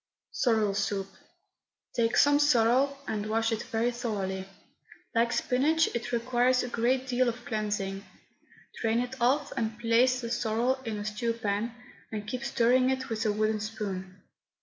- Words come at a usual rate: Yes, average, 155 wpm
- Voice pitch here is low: No, high, 230 Hz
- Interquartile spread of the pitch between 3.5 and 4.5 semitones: No, average, 2.7 semitones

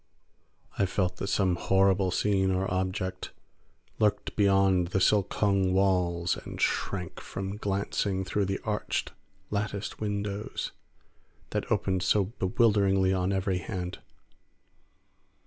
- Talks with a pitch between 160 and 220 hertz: No, very low, 95 Hz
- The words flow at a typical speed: No, slow, 115 wpm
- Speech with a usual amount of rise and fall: No, narrow, 1.5 semitones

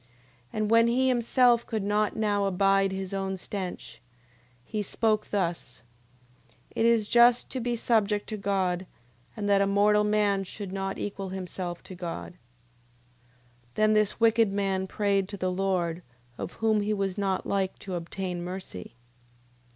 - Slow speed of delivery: No, average, 160 wpm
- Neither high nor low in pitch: No, high, 200 Hz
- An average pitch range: No, narrow, 2.2 semitones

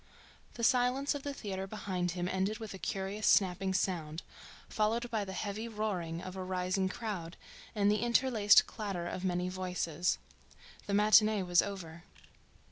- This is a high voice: Yes, high, 195 Hz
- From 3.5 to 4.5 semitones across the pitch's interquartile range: No, average, 3.0 semitones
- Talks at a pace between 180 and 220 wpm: No, average, 155 wpm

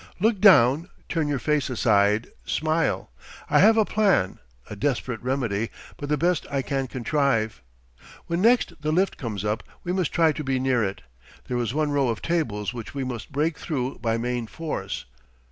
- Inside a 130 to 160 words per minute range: No, average, 180 wpm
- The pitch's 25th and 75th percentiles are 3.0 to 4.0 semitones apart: No, wide, 5.5 semitones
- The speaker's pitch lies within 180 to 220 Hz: No, low, 135 Hz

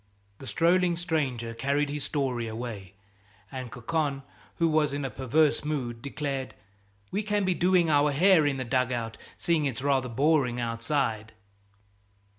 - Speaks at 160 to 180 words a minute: No, average, 150 wpm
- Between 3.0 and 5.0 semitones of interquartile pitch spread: Yes, average, 4.3 semitones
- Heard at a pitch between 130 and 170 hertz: Yes, medium, 140 Hz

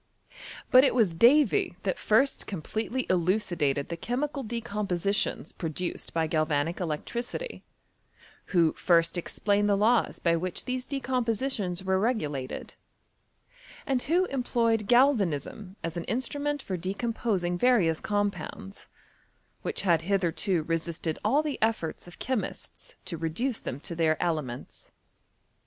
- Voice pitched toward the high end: Yes, high, 195 Hz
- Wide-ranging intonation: Yes, wide, 6.3 semitones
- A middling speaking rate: No, slow, 125 wpm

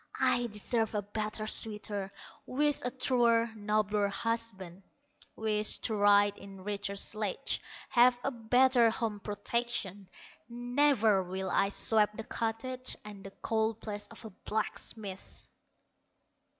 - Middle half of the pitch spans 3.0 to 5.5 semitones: No, narrow, 2.4 semitones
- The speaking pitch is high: Yes, high, 215 Hz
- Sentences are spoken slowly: Yes, slow, 125 wpm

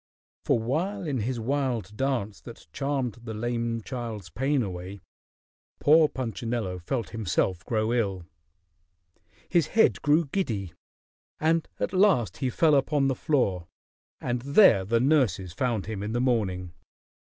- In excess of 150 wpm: No, average, 140 wpm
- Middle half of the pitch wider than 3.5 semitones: Yes, average, 5.3 semitones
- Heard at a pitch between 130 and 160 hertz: No, low, 120 Hz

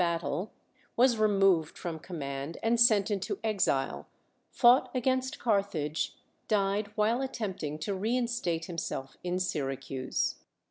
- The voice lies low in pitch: No, high, 195 Hz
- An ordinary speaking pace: No, slow, 120 wpm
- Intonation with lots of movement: Yes, wide, 6.0 semitones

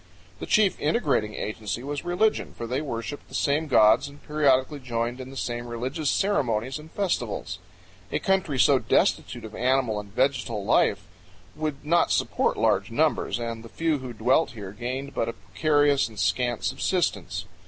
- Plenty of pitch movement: No, average, 4.4 semitones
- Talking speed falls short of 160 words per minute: No, average, 165 wpm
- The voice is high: No, low, 130 Hz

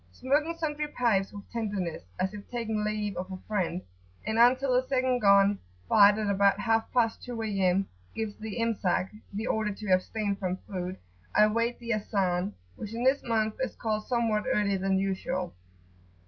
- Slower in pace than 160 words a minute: No, average, 175 wpm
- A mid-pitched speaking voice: No, high, 215 Hz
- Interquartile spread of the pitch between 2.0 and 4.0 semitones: Yes, average, 2.9 semitones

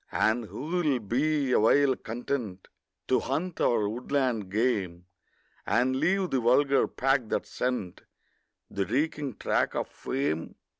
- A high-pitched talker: No, low, 125 Hz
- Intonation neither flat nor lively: Yes, average, 4.5 semitones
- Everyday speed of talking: No, slow, 130 wpm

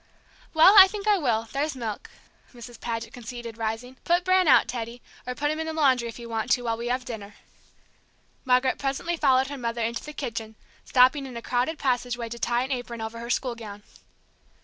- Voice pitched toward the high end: Yes, high, 245 Hz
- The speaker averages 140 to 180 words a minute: No, fast, 205 wpm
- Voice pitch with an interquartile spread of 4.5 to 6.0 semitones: No, average, 3.1 semitones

